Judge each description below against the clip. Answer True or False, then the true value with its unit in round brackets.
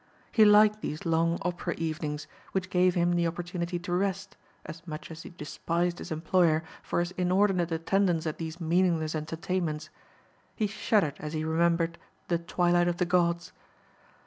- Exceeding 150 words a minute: True (160 wpm)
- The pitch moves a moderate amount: False (1.9 semitones)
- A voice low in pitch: False (170 Hz)